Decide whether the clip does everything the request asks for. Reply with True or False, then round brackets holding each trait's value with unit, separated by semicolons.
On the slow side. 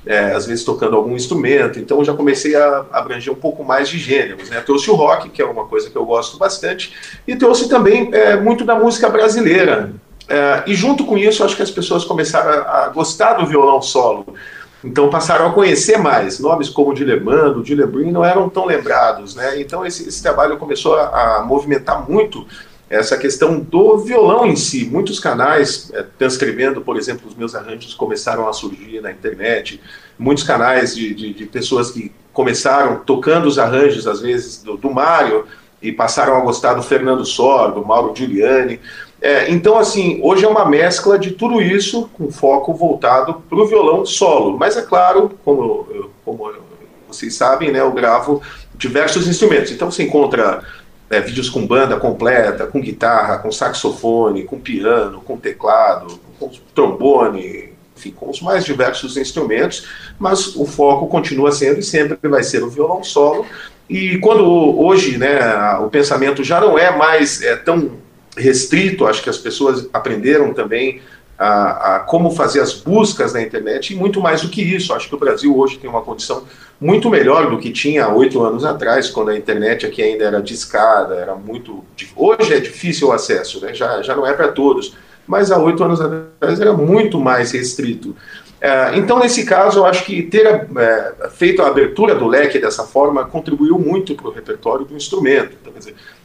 False (185 wpm)